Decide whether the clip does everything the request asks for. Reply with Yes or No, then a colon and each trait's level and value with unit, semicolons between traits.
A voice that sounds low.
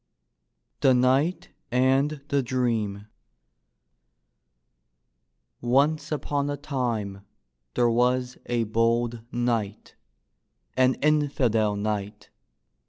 Yes: low, 125 Hz